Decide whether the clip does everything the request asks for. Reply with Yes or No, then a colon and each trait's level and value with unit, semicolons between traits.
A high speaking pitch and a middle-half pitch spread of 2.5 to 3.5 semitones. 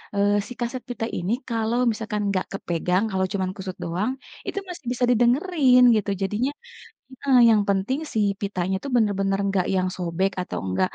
No: high, 205 Hz; average, 4.4 semitones